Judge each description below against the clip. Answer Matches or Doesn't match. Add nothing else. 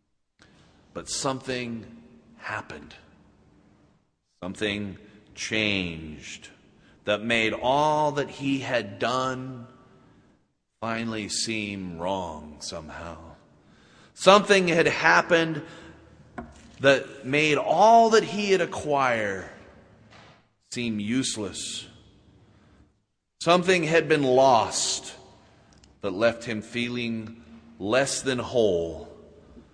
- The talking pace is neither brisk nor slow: Doesn't match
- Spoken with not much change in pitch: Doesn't match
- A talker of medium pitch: Doesn't match